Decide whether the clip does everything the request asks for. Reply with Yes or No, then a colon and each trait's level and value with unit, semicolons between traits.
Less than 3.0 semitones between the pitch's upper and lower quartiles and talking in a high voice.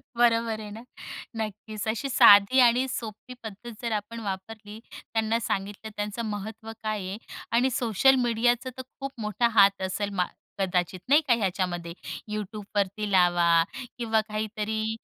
Yes: narrow, 2.6 semitones; high, 215 Hz